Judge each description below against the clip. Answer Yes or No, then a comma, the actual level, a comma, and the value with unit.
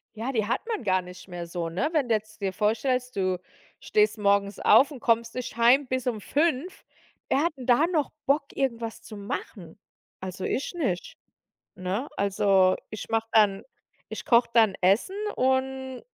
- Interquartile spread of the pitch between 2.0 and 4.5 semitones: No, average, 4.9 semitones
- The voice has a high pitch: Yes, high, 230 Hz